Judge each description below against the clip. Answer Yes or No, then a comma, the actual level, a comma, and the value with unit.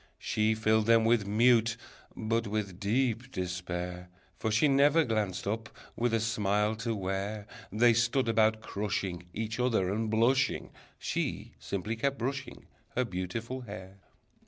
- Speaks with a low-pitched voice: Yes, low, 110 Hz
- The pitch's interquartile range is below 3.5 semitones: Yes, average, 2.7 semitones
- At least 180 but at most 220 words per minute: No, average, 140 wpm